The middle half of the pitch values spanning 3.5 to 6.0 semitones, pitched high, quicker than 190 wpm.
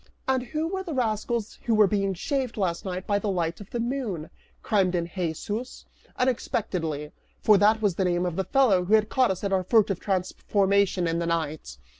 Yes: average, 4.1 semitones; high, 200 Hz; average, 200 wpm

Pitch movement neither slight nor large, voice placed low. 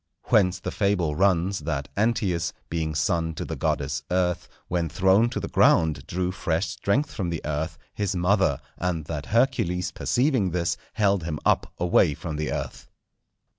Yes: average, 3.6 semitones; very low, 90 Hz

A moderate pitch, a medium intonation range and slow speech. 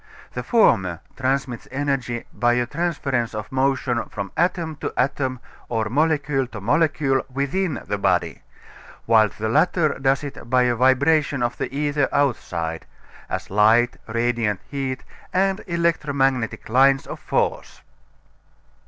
No: low, 130 Hz; average, 3.5 semitones; slow, 130 wpm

